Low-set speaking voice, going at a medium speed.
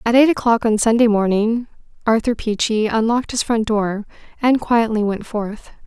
No: high, 225 Hz; average, 165 wpm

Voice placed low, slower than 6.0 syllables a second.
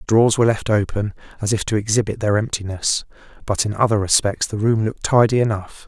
No: low, 105 Hz; 6.1 syllables/s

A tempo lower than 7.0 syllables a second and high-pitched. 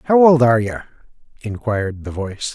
No: 6.0 syllables/s; low, 120 Hz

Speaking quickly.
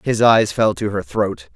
Yes: fast, 230 wpm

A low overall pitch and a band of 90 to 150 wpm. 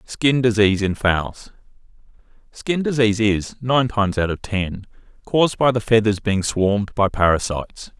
Yes: low, 110 Hz; average, 145 wpm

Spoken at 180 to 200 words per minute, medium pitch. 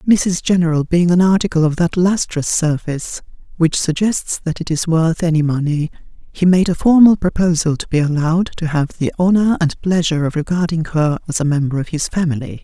Yes: average, 190 wpm; medium, 165 Hz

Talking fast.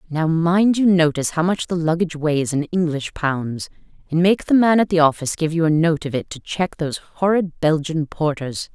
Yes: fast, 215 wpm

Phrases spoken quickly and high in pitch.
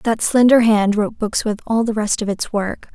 Yes: fast, 245 wpm; high, 215 Hz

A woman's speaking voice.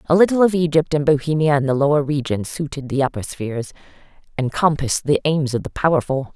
Yes: female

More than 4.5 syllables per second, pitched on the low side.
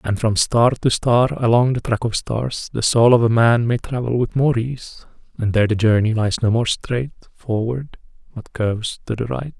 Yes: 4.8 syllables/s; low, 120 Hz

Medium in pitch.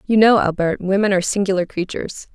No: high, 195 Hz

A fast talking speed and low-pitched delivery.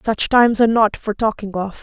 No: fast, 230 wpm; high, 215 Hz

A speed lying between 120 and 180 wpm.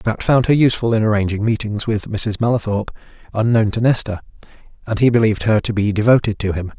No: average, 195 wpm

